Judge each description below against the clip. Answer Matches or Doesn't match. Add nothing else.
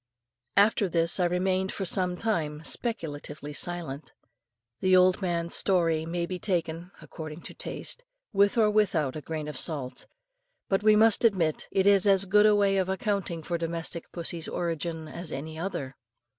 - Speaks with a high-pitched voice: Doesn't match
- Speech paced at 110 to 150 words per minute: Doesn't match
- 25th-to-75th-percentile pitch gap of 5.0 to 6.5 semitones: Doesn't match